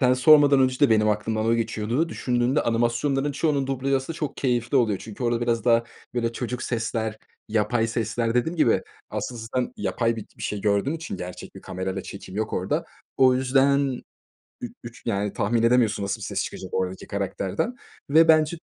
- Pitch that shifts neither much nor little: Yes, average, 3.6 semitones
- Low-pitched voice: Yes, low, 120 Hz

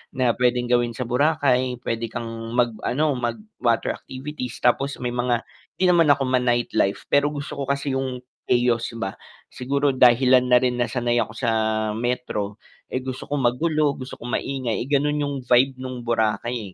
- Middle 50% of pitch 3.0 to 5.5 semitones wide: No, narrow, 2.4 semitones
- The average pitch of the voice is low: Yes, low, 125 Hz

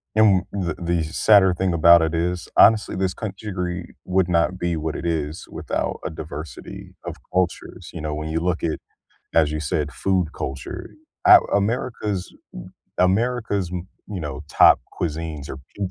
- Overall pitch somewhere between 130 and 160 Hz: No, very low, 85 Hz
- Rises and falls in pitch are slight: No, average, 3.3 semitones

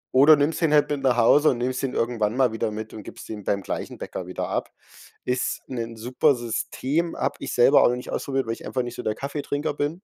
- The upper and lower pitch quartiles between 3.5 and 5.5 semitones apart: Yes, average, 3.8 semitones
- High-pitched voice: No, low, 125 Hz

